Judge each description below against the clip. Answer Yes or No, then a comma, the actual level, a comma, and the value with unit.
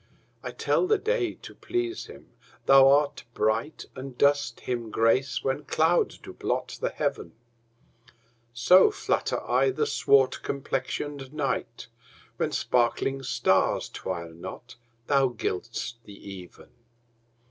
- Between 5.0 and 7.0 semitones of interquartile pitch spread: No, average, 4.2 semitones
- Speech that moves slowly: Yes, slow, 125 wpm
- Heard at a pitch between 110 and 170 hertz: Yes, low, 135 Hz